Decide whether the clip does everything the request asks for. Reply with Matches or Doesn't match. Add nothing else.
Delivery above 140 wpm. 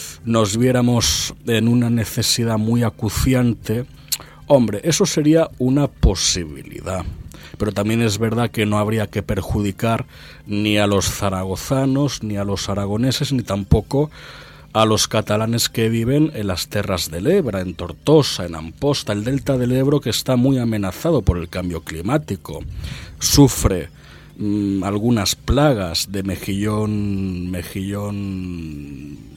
Doesn't match